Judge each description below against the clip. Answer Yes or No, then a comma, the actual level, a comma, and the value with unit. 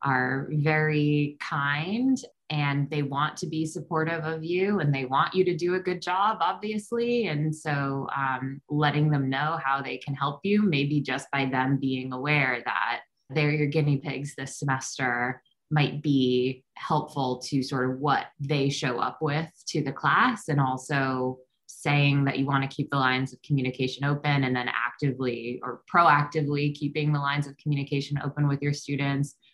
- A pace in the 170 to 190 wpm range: Yes, average, 175 wpm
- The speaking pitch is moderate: Yes, medium, 145 Hz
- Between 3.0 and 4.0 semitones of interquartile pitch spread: No, narrow, 2.4 semitones